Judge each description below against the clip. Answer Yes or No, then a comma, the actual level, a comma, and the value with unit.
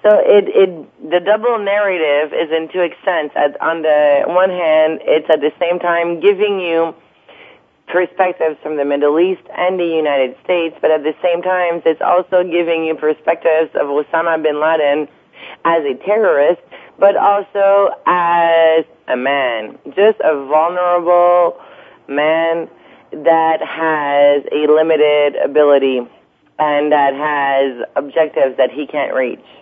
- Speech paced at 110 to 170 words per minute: Yes, average, 140 wpm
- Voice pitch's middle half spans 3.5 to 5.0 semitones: No, average, 2.9 semitones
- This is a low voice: No, medium, 160 Hz